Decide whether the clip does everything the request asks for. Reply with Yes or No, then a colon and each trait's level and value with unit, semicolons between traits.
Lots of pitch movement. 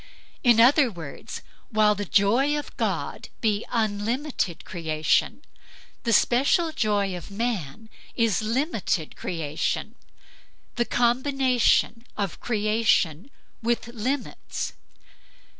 No: average, 3.6 semitones